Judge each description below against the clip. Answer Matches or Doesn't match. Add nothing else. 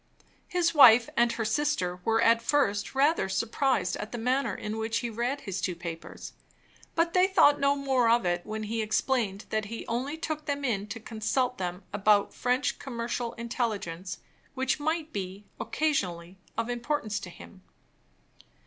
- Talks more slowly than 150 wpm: Doesn't match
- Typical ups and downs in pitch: Matches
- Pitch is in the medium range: Doesn't match